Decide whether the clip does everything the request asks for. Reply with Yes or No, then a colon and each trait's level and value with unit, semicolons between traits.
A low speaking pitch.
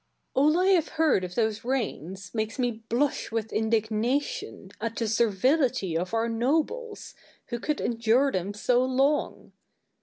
No: high, 235 Hz